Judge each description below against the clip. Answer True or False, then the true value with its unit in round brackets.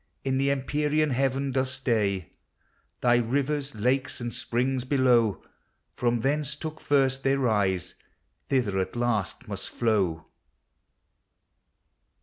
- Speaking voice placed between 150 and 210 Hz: False (130 Hz)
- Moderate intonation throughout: True (3.5 semitones)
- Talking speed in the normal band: False (115 wpm)